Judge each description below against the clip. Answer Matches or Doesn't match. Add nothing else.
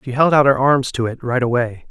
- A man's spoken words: Matches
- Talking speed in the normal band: Doesn't match